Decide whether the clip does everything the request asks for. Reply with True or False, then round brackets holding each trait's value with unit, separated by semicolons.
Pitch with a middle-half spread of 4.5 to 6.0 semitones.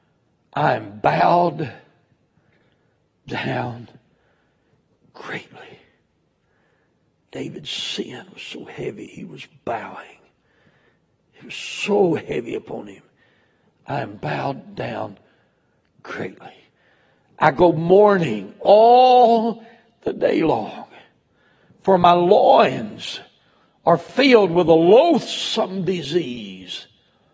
True (5.1 semitones)